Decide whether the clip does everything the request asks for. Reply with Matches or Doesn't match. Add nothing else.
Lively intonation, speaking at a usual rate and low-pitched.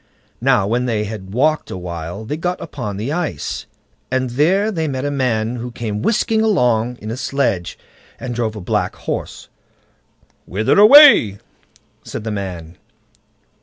Matches